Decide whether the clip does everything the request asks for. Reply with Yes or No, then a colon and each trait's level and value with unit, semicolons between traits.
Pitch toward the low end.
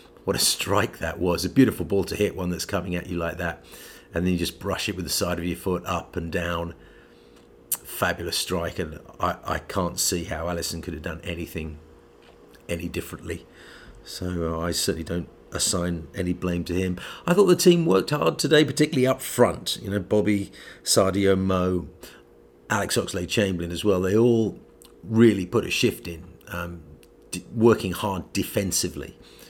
Yes: very low, 90 Hz